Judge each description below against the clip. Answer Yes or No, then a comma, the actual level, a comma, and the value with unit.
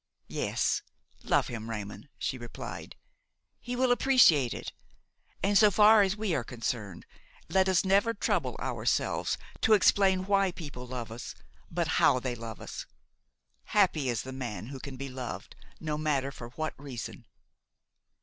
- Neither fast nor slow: Yes, average, 150 wpm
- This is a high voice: No, medium, 140 Hz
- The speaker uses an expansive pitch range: Yes, wide, 8.1 semitones